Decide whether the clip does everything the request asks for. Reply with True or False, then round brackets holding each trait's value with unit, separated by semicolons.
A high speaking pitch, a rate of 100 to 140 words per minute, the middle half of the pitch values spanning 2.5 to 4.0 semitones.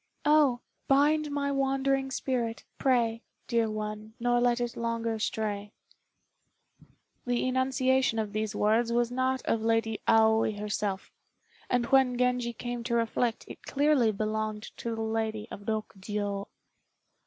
True (230 Hz; 135 wpm; 2.9 semitones)